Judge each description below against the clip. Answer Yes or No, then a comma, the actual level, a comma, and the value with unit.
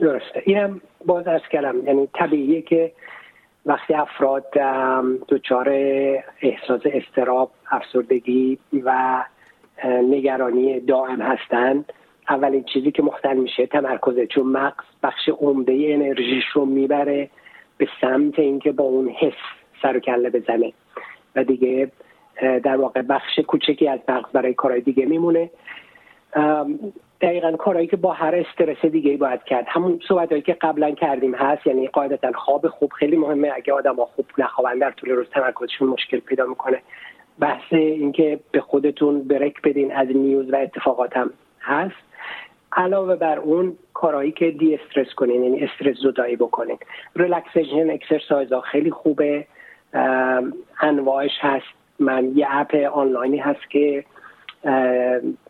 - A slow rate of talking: No, average, 135 wpm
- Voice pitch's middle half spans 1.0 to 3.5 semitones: Yes, average, 2.8 semitones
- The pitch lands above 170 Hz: No, medium, 140 Hz